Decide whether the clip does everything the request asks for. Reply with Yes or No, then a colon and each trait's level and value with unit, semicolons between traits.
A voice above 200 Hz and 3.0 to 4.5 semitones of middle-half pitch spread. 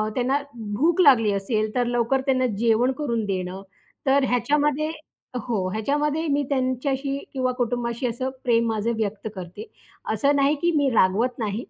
Yes: high, 245 Hz; average, 4.0 semitones